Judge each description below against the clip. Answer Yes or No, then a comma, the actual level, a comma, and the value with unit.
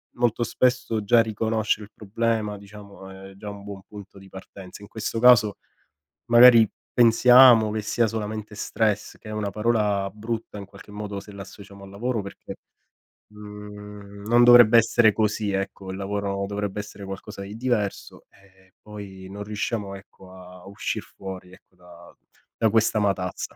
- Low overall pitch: Yes, low, 105 Hz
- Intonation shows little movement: Yes, narrow, 2.1 semitones